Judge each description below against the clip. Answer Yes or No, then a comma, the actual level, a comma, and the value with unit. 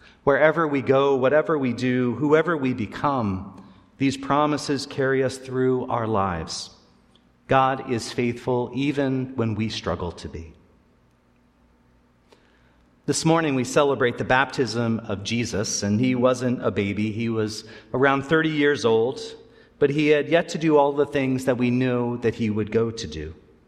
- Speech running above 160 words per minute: No, average, 155 wpm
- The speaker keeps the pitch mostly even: No, wide, 5.4 semitones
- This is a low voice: Yes, low, 125 Hz